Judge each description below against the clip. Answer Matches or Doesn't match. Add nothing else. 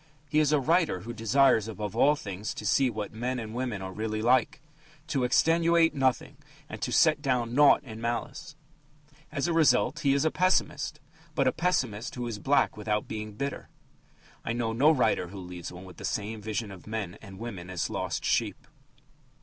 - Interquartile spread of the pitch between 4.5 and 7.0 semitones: Matches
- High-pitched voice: Doesn't match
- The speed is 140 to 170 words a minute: Doesn't match